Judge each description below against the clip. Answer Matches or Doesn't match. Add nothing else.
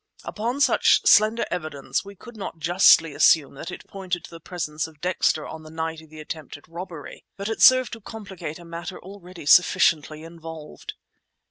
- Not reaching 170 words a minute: Doesn't match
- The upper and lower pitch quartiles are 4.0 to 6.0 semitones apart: Doesn't match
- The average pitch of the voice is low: Doesn't match